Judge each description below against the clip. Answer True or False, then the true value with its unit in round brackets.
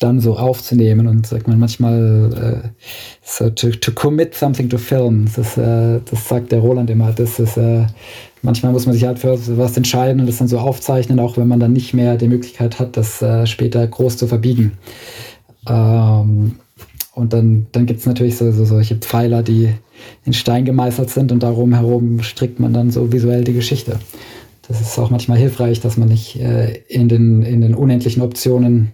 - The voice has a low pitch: True (120 Hz)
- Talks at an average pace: False (195 wpm)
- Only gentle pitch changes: True (1.3 semitones)